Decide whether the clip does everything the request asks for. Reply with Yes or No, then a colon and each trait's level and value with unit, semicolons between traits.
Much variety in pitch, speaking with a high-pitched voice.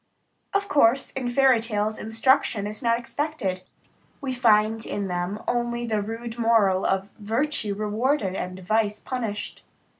No: average, 2.9 semitones; high, 225 Hz